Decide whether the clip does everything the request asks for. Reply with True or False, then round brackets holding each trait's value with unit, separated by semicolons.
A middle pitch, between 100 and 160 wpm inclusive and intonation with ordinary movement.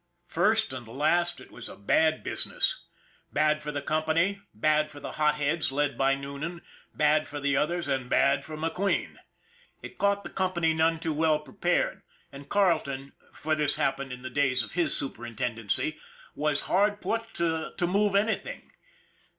False (155 Hz; 170 wpm; 3.7 semitones)